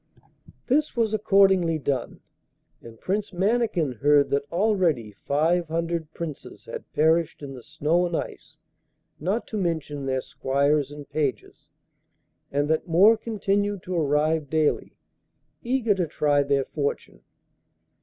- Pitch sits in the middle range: Yes, medium, 160 Hz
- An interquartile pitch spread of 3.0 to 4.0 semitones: No, average, 5.1 semitones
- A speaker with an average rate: No, slow, 130 wpm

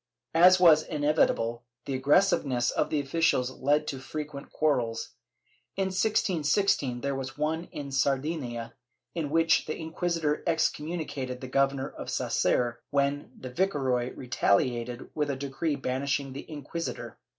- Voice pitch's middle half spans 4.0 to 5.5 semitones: No, average, 3.5 semitones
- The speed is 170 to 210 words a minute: No, average, 140 wpm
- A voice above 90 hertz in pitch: Yes, medium, 140 Hz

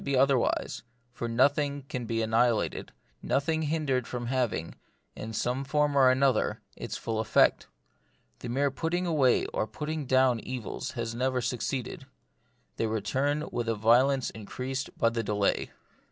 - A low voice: Yes, low, 130 Hz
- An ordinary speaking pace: Yes, average, 155 wpm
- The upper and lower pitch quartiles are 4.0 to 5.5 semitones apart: No, average, 3.3 semitones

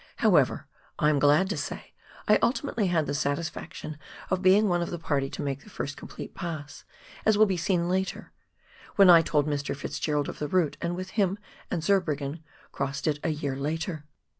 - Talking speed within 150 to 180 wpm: No, average, 195 wpm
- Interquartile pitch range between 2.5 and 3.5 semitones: No, average, 4.2 semitones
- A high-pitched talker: No, medium, 160 Hz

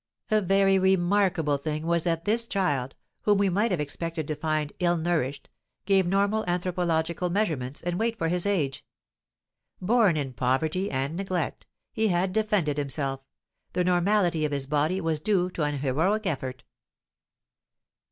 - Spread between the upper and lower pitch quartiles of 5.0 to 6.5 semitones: No, average, 4.4 semitones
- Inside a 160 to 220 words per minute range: No, average, 150 wpm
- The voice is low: No, medium, 175 Hz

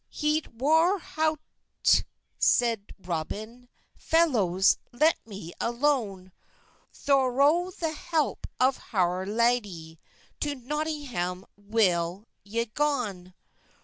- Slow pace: Yes, slow, 85 wpm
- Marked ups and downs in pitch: Yes, wide, 7.6 semitones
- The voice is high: Yes, high, 240 Hz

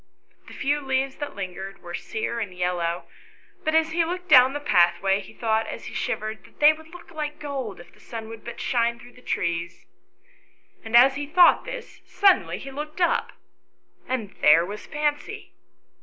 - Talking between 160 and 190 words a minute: Yes, average, 185 wpm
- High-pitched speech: Yes, very high, 255 Hz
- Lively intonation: Yes, wide, 6.8 semitones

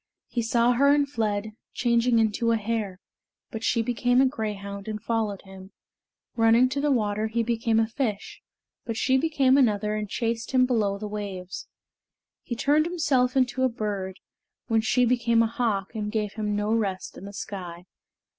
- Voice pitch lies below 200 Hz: No, high, 225 Hz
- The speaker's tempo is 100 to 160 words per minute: No, average, 175 wpm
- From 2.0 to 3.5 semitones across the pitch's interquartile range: Yes, average, 3.0 semitones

